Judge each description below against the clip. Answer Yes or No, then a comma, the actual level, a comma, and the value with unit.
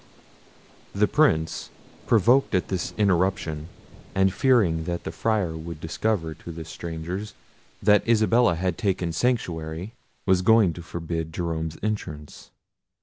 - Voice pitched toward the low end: Yes, very low, 90 Hz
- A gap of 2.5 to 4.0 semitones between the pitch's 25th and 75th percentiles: No, average, 4.6 semitones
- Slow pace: Yes, slow, 125 wpm